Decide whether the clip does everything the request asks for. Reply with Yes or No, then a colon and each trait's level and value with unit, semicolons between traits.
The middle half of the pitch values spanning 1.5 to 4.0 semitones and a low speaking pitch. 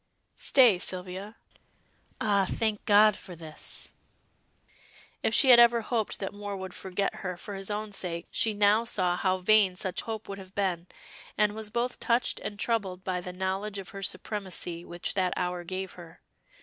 No: average, 2.7 semitones; high, 195 Hz